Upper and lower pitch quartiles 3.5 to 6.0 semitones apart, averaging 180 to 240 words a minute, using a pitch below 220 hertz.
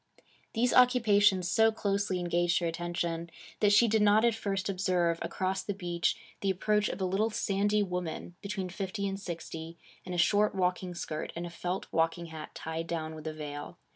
No: average, 3.1 semitones; average, 185 wpm; medium, 185 Hz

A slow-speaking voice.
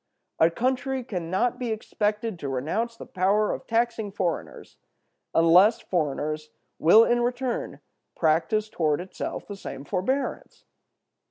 Yes: slow, 125 wpm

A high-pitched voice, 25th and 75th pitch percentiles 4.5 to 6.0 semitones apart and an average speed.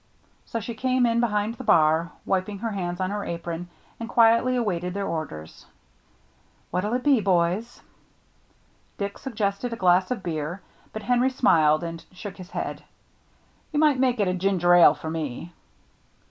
Yes: high, 200 Hz; average, 5.1 semitones; average, 150 wpm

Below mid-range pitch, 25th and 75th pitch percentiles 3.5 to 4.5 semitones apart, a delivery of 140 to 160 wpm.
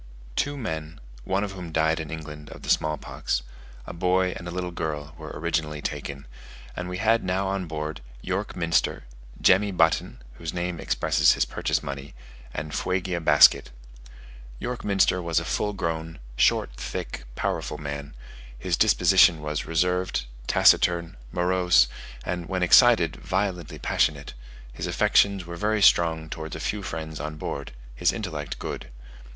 No: very low, 85 Hz; average, 3.1 semitones; average, 155 wpm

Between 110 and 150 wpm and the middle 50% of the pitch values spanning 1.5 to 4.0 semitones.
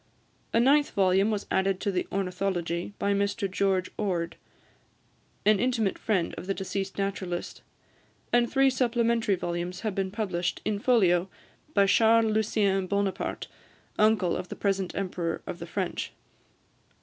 Yes: average, 140 wpm; average, 2.8 semitones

